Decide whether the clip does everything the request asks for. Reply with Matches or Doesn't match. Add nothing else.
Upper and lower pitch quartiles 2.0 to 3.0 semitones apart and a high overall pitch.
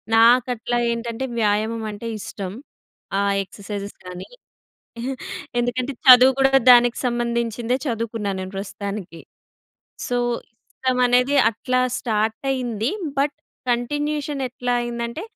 Matches